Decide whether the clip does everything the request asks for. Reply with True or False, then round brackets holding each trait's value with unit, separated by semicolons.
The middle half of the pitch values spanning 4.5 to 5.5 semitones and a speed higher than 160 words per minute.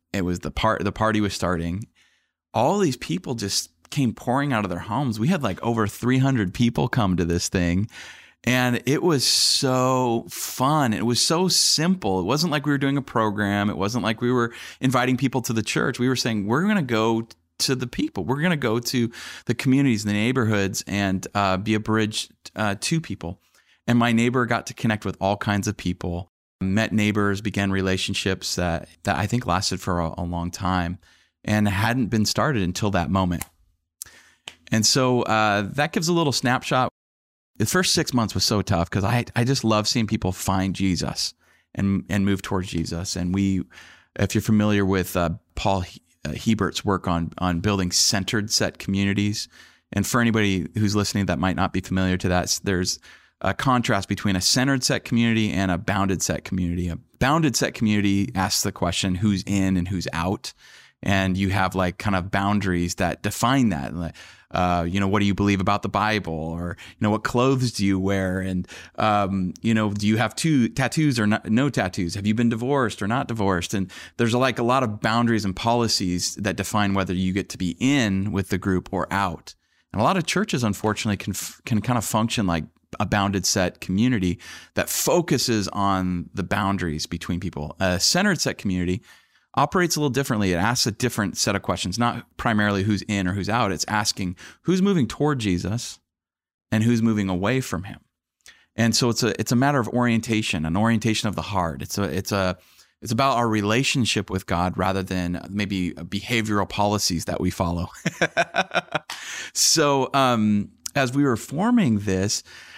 False (4.1 semitones; 195 wpm)